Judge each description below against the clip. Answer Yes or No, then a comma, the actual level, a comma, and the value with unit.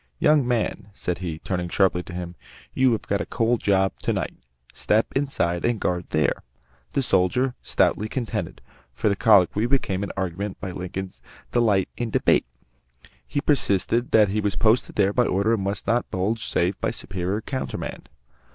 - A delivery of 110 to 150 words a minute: No, average, 175 wpm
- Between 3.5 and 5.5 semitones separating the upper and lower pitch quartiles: Yes, average, 4.1 semitones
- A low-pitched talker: Yes, low, 100 Hz